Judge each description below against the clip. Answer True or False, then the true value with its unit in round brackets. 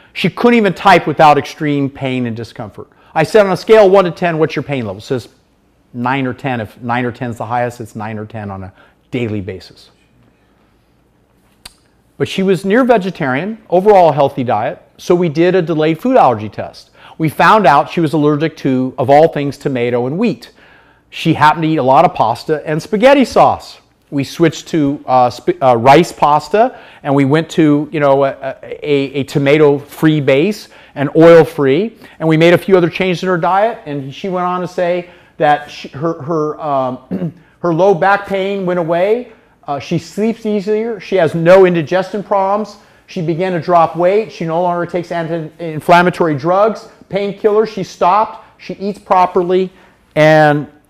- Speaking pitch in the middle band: True (165 Hz)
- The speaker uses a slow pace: False (185 wpm)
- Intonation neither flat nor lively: True (4.8 semitones)